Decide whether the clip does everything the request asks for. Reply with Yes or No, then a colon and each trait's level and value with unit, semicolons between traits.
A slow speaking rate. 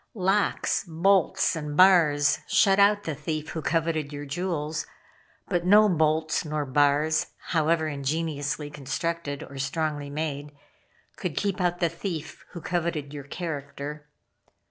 Yes: slow, 130 wpm